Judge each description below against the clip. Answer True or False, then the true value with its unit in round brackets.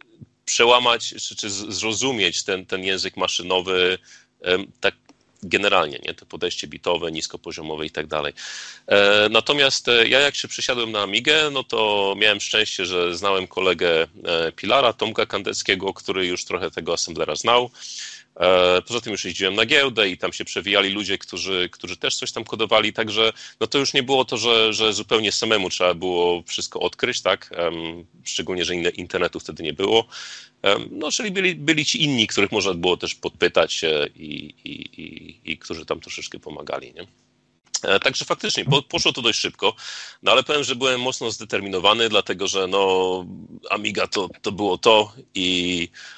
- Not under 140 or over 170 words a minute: True (160 wpm)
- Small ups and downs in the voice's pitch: False (5.4 semitones)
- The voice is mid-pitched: False (100 Hz)